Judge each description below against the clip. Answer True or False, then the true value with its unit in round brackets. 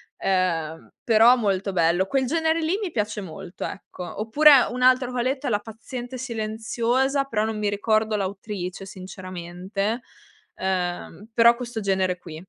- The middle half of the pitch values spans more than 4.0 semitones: True (4.7 semitones)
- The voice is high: True (215 Hz)